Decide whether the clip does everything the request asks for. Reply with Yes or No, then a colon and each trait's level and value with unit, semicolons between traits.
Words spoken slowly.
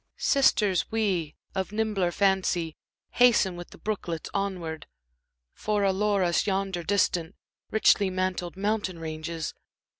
Yes: slow, 115 wpm